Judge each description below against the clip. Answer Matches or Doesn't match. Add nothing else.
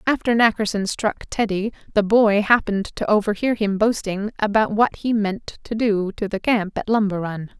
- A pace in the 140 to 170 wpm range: Doesn't match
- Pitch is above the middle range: Matches